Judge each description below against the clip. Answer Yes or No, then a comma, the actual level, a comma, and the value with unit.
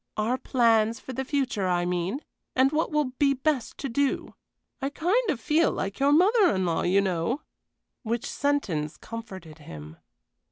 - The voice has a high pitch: Yes, high, 240 Hz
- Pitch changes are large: Yes, wide, 7.3 semitones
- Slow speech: No, average, 165 wpm